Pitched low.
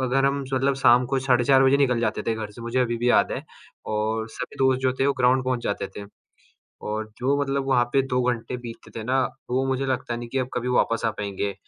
Yes: low, 125 Hz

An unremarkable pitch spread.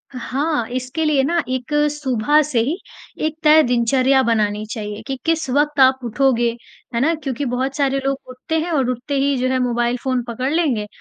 Yes: average, 3.2 semitones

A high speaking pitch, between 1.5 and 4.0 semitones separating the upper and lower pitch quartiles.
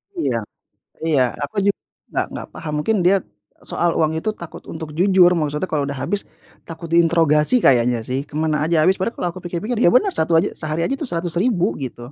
No: medium, 170 Hz; average, 3.5 semitones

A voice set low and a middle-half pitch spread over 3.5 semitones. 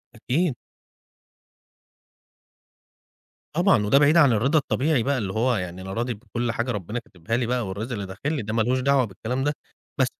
Yes: low, 120 Hz; average, 4.5 semitones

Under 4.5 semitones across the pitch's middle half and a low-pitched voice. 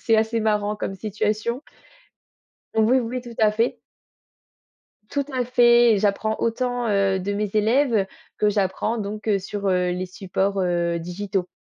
No: average, 2.9 semitones; high, 210 Hz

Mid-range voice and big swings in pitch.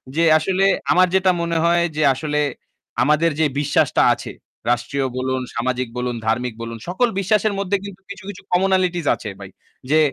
Yes: medium, 165 Hz; wide, 6.4 semitones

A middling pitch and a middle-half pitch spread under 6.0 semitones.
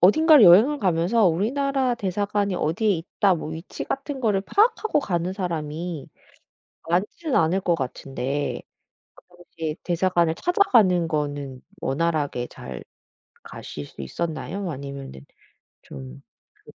Yes: medium, 175 Hz; wide, 5.5 semitones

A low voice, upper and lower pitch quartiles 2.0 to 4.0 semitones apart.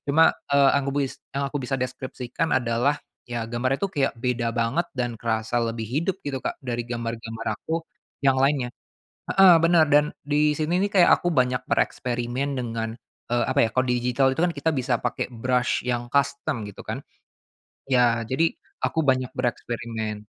Yes: low, 130 Hz; average, 3.1 semitones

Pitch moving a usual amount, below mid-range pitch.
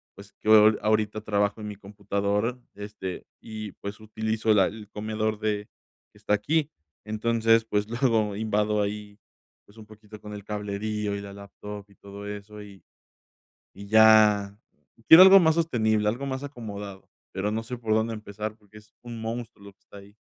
No: narrow, 1.4 semitones; low, 105 Hz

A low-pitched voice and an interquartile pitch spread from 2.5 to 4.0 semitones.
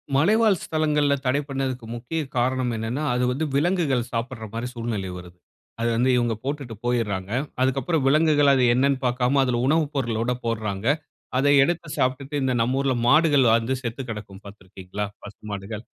Yes: low, 125 Hz; average, 3.6 semitones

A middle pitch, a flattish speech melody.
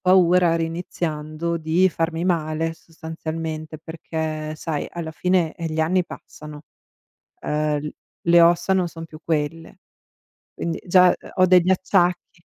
Yes: medium, 165 Hz; narrow, 1.8 semitones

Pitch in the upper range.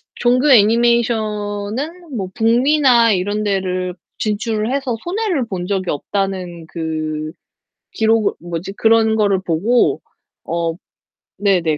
Yes: high, 210 Hz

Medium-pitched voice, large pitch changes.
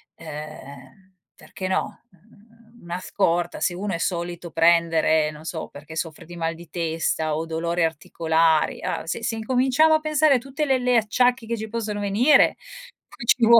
Yes: medium, 180 Hz; wide, 6.0 semitones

